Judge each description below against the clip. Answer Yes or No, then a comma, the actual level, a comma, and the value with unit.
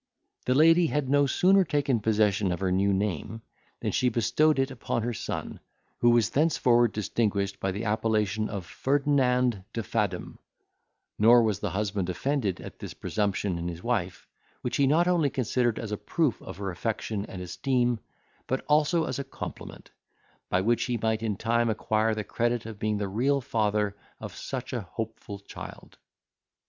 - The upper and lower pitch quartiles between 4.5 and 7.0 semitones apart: No, average, 4.1 semitones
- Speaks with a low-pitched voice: Yes, low, 115 Hz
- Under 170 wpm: No, average, 175 wpm